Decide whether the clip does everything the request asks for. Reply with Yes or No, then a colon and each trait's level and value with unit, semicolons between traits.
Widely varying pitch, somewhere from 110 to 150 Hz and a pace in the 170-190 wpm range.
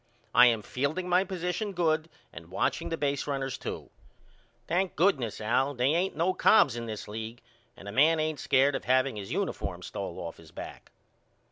Yes: wide, 5.9 semitones; medium, 140 Hz; average, 175 wpm